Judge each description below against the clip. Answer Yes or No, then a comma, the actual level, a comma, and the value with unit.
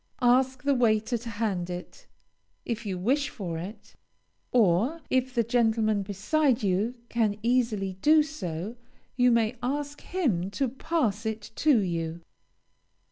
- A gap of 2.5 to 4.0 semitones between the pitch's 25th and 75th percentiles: No, average, 4.7 semitones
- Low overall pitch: No, high, 225 Hz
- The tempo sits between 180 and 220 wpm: No, slow, 135 wpm